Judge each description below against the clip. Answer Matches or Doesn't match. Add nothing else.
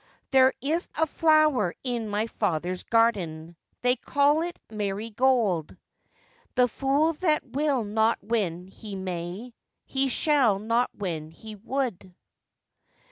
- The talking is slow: Matches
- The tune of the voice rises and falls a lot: Matches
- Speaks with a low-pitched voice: Doesn't match